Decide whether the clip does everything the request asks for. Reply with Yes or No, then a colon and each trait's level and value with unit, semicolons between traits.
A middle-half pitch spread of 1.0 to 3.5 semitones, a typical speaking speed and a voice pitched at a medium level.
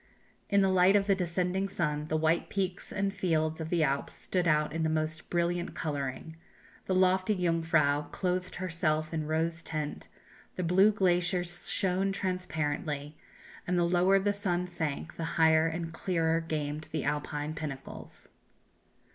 Yes: average, 2.7 semitones; average, 155 wpm; medium, 170 Hz